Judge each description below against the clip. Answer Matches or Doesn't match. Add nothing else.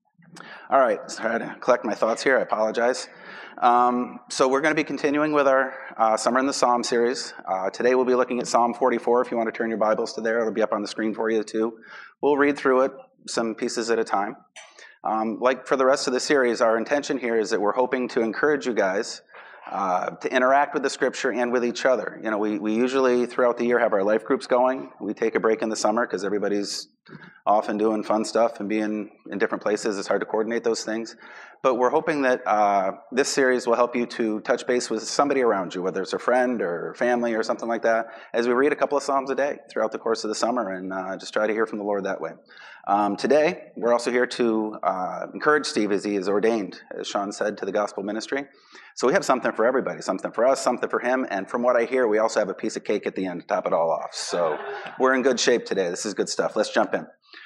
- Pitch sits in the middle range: Doesn't match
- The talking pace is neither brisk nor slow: Doesn't match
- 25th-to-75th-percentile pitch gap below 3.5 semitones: Matches